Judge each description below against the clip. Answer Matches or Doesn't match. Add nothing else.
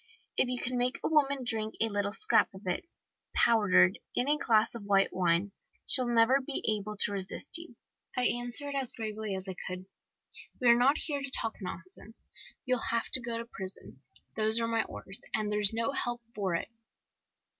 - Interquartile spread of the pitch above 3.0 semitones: Matches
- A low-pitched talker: Doesn't match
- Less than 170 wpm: Doesn't match